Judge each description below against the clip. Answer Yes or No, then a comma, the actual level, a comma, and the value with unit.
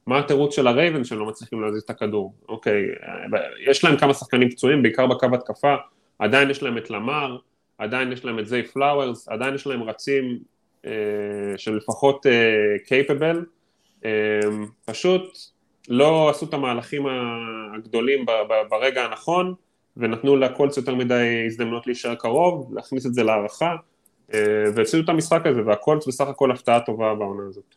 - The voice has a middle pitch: No, low, 125 Hz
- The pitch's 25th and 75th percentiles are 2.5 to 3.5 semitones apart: No, average, 4.2 semitones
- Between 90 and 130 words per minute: No, fast, 150 wpm